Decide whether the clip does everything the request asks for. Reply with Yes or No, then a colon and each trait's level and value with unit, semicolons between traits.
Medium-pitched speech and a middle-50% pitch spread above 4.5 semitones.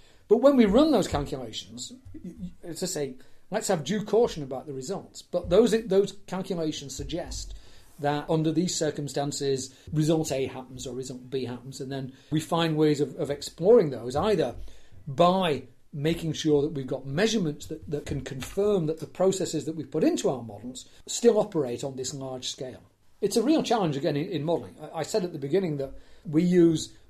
Yes: medium, 150 Hz; average, 5.1 semitones